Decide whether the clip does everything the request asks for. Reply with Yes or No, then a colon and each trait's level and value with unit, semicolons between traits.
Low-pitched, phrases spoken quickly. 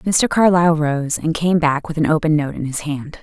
No: medium, 155 Hz; fast, 240 wpm